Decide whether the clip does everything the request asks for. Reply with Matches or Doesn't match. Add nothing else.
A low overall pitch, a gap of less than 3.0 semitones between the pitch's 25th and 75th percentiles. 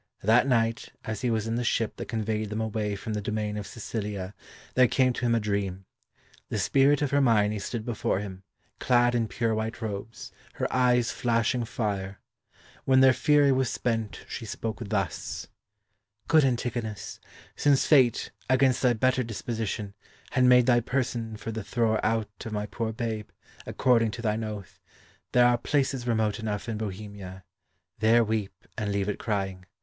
Matches